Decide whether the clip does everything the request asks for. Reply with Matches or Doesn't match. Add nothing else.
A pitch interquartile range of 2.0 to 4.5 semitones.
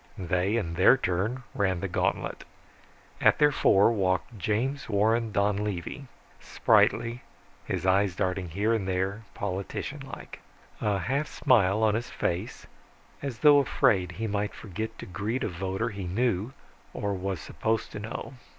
Matches